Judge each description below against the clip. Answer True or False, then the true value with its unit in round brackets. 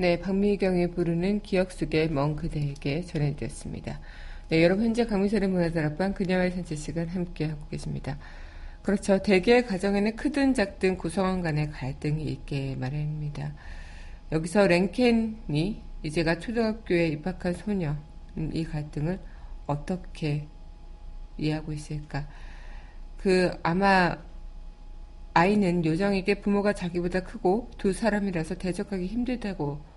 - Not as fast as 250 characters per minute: False (300 characters per minute)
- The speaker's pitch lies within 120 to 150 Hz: False (170 Hz)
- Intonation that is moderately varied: True (4.7 semitones)